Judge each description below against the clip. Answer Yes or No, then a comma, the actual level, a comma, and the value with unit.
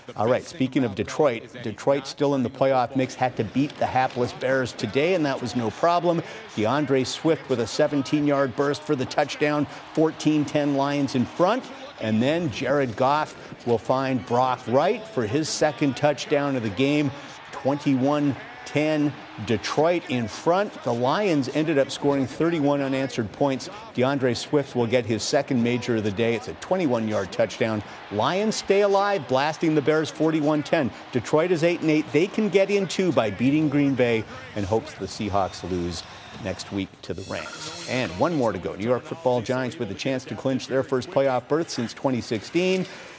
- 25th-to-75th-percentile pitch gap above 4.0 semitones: No, average, 3.7 semitones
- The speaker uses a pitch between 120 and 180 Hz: Yes, low, 135 Hz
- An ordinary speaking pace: Yes, average, 180 wpm